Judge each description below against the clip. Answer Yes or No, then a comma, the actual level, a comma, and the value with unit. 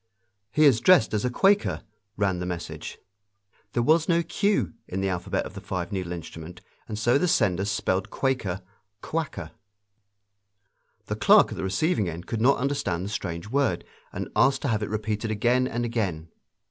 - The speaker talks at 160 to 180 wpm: Yes, average, 175 wpm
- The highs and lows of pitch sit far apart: Yes, wide, 5.9 semitones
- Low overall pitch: Yes, low, 105 Hz